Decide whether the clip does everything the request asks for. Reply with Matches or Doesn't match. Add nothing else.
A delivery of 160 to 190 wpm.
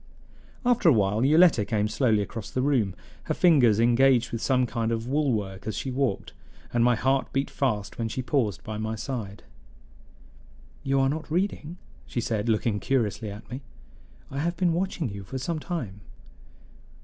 Matches